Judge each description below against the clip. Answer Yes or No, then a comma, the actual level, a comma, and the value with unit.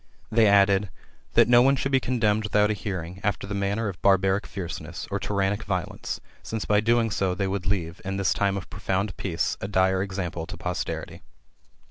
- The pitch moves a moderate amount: No, narrow, 1.8 semitones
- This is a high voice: No, low, 100 Hz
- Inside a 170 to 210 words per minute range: Yes, average, 195 wpm